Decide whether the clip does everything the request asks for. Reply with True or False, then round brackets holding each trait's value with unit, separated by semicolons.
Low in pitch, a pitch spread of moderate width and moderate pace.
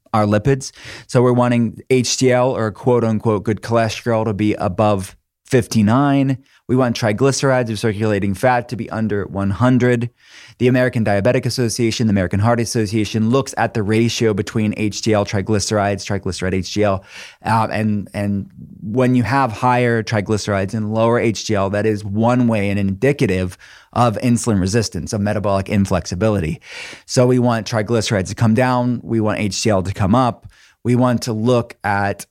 True (110 Hz; 3.0 semitones; 155 wpm)